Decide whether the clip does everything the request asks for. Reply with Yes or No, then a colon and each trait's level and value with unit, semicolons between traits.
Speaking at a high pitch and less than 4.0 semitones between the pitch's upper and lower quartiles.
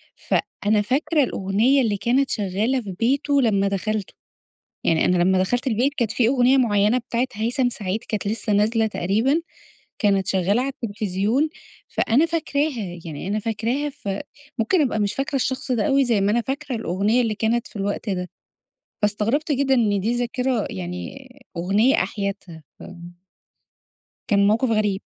No: high, 225 Hz; average, 4.4 semitones